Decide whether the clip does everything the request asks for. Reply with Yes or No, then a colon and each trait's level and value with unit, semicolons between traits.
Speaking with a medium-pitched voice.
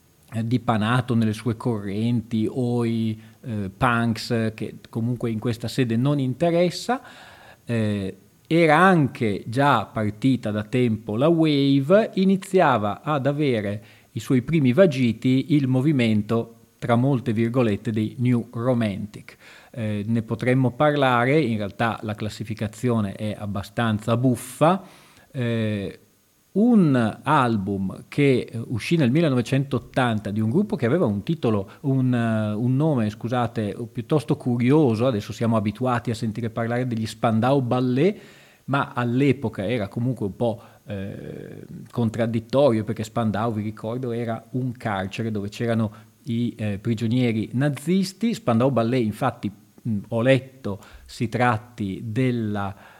No: low, 120 Hz